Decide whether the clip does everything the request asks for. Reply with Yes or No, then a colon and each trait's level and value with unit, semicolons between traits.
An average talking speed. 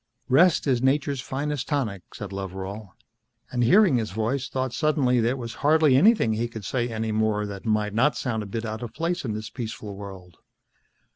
Yes: average, 190 wpm